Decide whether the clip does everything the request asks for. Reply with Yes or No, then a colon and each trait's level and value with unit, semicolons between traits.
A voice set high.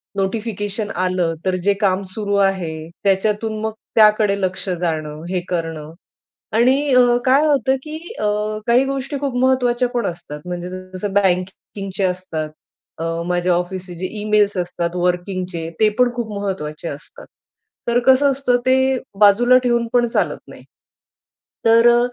Yes: high, 200 Hz